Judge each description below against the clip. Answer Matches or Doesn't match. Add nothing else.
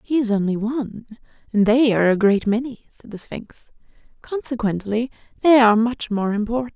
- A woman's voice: Matches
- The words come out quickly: Doesn't match